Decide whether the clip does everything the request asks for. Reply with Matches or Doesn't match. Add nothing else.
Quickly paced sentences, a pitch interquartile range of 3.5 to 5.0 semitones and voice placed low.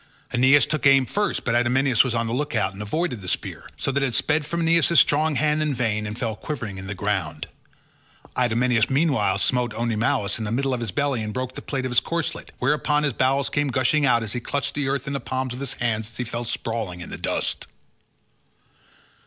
Matches